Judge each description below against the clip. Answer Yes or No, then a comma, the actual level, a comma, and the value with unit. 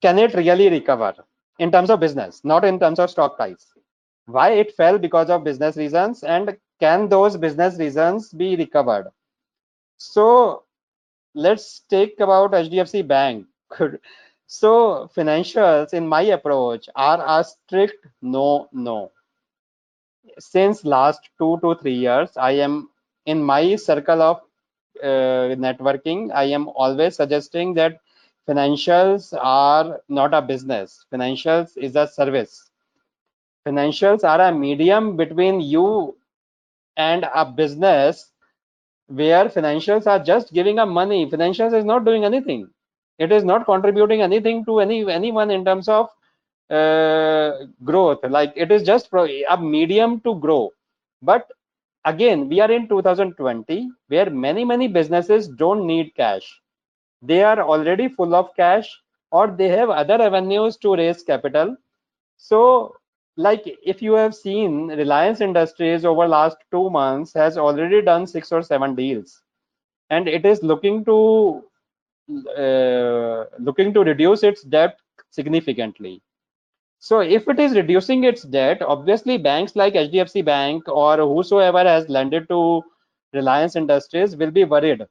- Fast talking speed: Yes, fast, 135 wpm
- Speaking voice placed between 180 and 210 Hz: No, medium, 170 Hz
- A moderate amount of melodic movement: No, wide, 5.7 semitones